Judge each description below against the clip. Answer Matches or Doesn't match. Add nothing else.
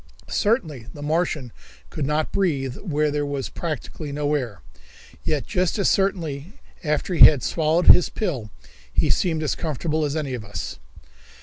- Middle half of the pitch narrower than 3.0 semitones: Doesn't match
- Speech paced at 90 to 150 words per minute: Doesn't match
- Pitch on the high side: Doesn't match